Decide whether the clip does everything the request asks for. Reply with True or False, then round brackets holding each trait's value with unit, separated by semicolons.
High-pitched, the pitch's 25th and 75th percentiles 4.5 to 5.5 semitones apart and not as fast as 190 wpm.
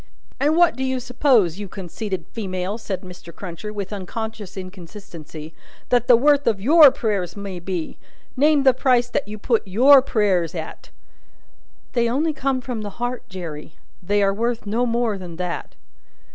True (210 Hz; 5.2 semitones; 165 wpm)